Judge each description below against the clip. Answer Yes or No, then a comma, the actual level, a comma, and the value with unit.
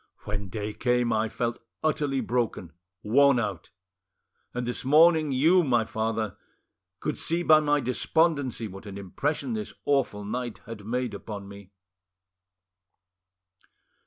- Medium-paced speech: No, slow, 130 wpm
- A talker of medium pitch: No, low, 120 Hz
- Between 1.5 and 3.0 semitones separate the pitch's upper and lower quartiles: No, average, 5.3 semitones